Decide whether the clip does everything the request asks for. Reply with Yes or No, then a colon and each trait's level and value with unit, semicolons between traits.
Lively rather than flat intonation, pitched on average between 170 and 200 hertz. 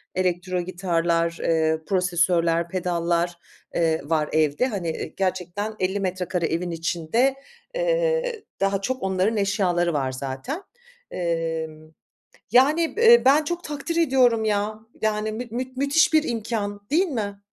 Yes: wide, 6.8 semitones; high, 190 Hz